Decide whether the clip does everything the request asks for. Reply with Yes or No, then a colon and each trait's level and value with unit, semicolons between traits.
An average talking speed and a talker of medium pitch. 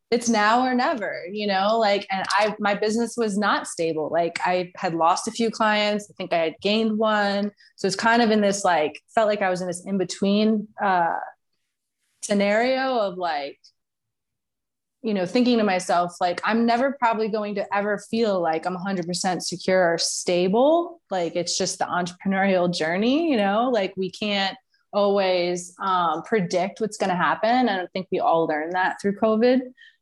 No: average, 185 wpm; high, 200 Hz